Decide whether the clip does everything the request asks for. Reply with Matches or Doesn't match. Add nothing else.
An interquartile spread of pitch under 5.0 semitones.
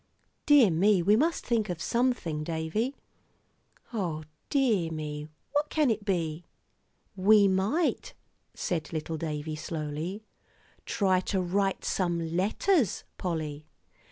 Doesn't match